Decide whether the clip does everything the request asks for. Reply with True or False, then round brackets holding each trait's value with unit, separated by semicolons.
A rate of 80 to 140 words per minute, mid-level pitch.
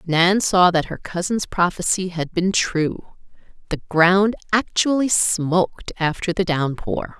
True (135 wpm; 180 Hz)